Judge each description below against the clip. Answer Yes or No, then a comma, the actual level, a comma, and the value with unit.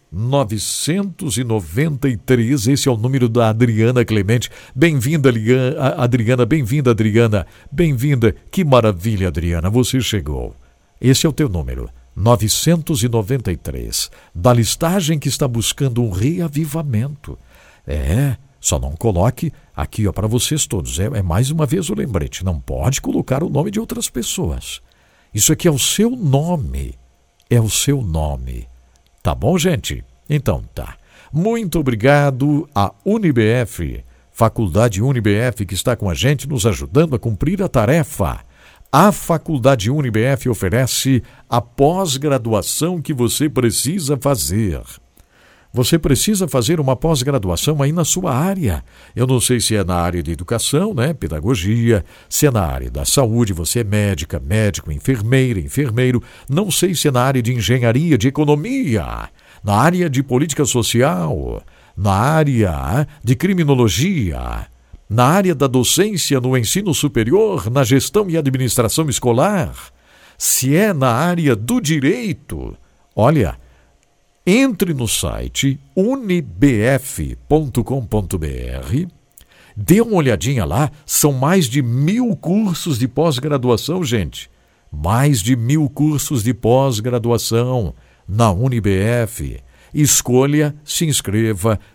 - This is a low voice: Yes, low, 125 Hz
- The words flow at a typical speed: No, slow, 125 wpm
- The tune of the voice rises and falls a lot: Yes, wide, 6.1 semitones